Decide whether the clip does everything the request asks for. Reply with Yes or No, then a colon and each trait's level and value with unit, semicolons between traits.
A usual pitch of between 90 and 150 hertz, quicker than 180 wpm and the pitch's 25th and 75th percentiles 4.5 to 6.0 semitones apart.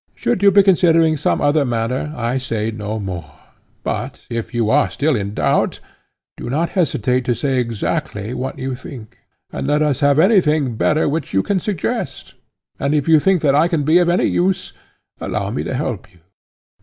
Yes: medium, 140 Hz; average, 190 wpm; wide, 5.5 semitones